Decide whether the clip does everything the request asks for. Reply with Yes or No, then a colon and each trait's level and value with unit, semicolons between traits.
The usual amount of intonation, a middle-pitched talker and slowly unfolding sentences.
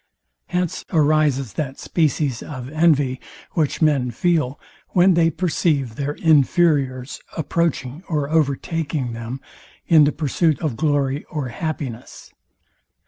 Yes: average, 3.3 semitones; medium, 150 Hz; slow, 115 wpm